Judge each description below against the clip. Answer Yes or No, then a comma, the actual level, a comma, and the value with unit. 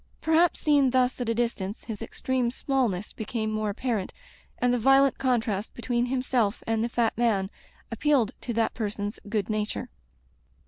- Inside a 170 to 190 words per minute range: No, average, 155 wpm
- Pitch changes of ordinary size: Yes, average, 3.0 semitones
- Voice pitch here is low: No, high, 235 Hz